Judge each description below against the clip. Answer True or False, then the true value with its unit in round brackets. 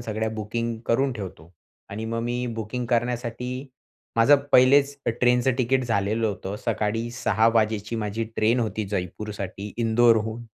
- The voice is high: False (115 Hz)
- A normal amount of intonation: False (2.1 semitones)